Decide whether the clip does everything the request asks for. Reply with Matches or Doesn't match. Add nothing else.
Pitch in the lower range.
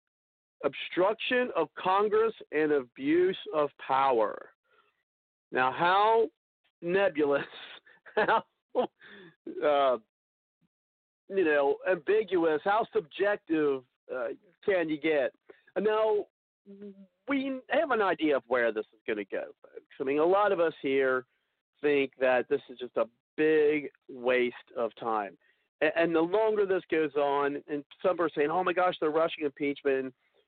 Doesn't match